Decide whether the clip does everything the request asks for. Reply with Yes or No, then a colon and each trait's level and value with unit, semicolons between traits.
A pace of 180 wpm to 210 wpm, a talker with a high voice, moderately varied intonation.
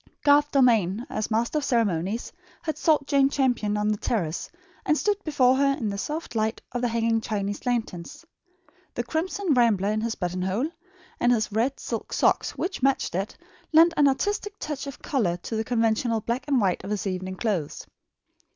Yes: average, 185 wpm; high, 235 Hz; average, 5.0 semitones